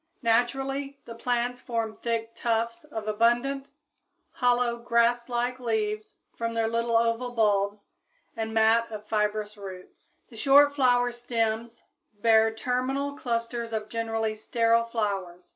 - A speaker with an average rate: No, slow, 125 wpm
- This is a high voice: Yes, high, 230 Hz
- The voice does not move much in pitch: Yes, narrow, 1.8 semitones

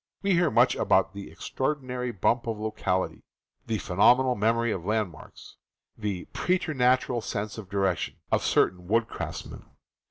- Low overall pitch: Yes, low, 110 Hz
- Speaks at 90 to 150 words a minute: Yes, average, 145 wpm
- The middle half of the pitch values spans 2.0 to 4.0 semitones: No, average, 4.4 semitones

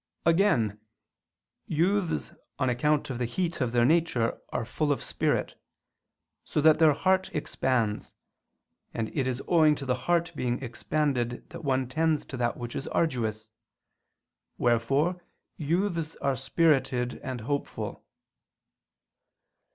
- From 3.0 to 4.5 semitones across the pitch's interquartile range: No, average, 5.0 semitones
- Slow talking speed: Yes, slow, 130 wpm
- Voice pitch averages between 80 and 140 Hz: Yes, low, 135 Hz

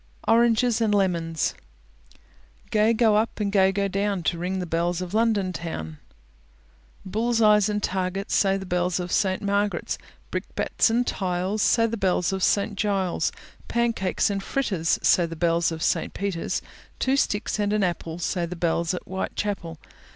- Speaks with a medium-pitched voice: No, high, 195 Hz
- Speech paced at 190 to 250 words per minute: No, average, 165 wpm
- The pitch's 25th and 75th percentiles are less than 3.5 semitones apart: Yes, average, 3.1 semitones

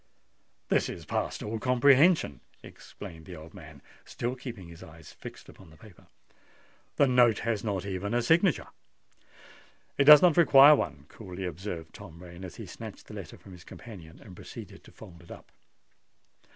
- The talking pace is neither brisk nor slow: Yes, average, 170 wpm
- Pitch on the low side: Yes, low, 100 Hz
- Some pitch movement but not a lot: No, wide, 6.3 semitones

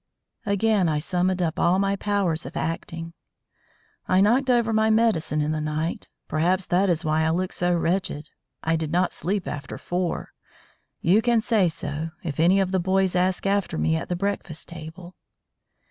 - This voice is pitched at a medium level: Yes, medium, 180 Hz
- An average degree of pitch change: Yes, average, 3.5 semitones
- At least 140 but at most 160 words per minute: No, average, 175 wpm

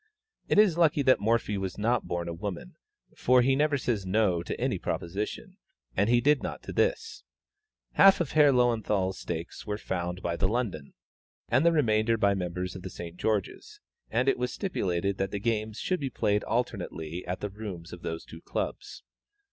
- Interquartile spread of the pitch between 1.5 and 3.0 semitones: No, wide, 5.4 semitones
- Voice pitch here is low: Yes, low, 105 Hz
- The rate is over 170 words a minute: Yes, average, 190 wpm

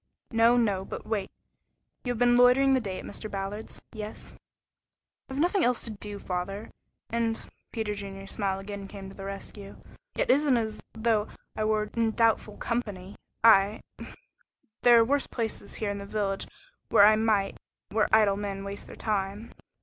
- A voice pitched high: Yes, high, 215 Hz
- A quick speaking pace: No, average, 175 wpm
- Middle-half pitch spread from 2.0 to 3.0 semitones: Yes, narrow, 2.6 semitones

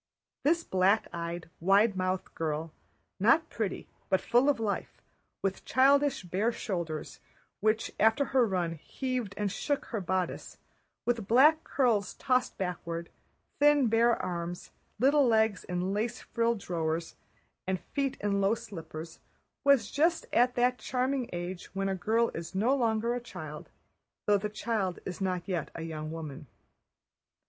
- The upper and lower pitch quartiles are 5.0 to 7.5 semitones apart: Yes, wide, 5.4 semitones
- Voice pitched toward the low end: No, high, 205 Hz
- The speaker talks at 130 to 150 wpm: Yes, average, 140 wpm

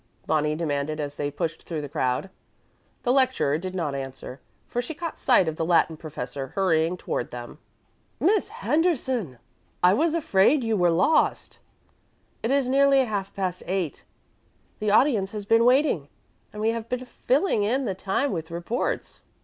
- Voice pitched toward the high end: Yes, high, 195 Hz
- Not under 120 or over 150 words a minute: No, average, 165 wpm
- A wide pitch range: Yes, wide, 8.3 semitones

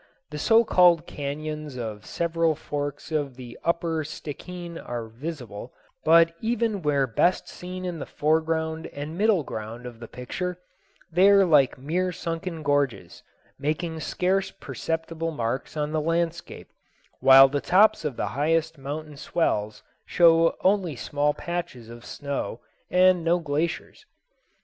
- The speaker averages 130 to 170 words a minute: Yes, average, 140 wpm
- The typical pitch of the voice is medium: Yes, medium, 160 Hz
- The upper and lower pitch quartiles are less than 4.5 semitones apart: Yes, average, 3.6 semitones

